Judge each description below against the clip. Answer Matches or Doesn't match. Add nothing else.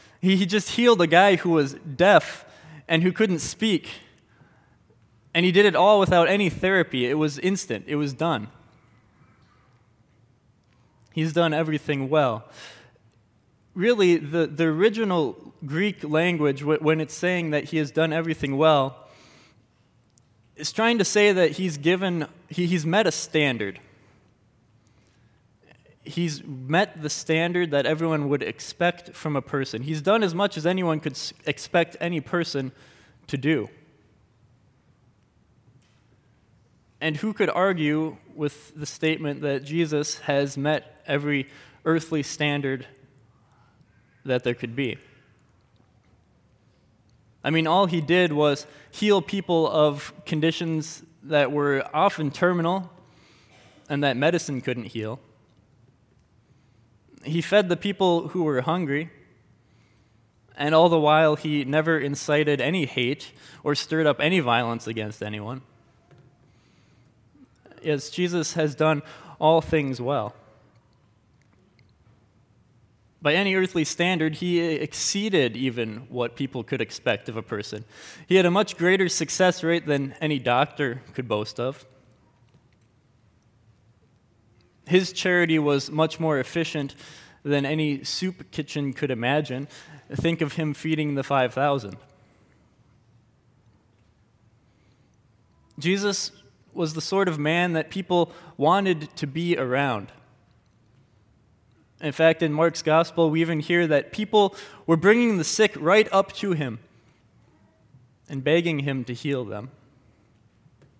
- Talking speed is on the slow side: Matches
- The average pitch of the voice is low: Doesn't match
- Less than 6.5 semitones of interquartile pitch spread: Matches